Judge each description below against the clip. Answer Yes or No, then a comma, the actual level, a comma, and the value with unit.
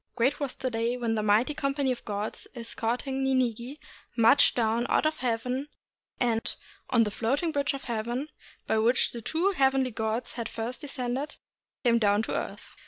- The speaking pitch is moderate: No, high, 245 Hz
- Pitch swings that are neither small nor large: Yes, average, 3.0 semitones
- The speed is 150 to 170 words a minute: No, average, 180 wpm